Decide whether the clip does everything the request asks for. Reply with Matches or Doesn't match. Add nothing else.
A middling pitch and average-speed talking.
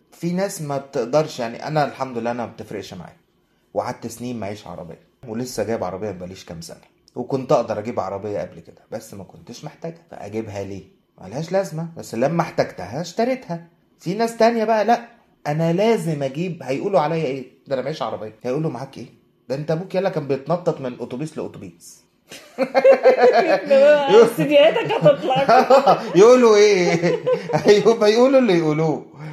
Doesn't match